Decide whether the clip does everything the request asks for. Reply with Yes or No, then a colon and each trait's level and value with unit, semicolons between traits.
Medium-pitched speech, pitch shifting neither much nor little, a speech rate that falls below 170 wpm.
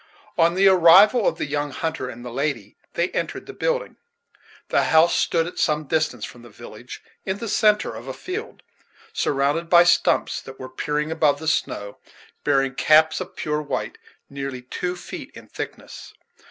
No: medium, 155 Hz; average, 4.4 semitones; average, 175 wpm